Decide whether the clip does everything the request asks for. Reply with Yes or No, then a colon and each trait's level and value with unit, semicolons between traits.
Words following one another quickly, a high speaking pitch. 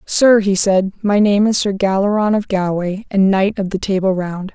Yes: fast, 210 wpm; high, 195 Hz